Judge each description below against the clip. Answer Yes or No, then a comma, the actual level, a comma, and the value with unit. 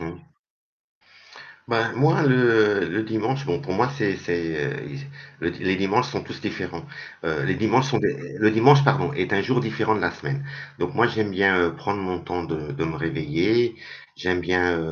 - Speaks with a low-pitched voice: Yes, low, 110 Hz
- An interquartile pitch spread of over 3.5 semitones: Yes, wide, 5.4 semitones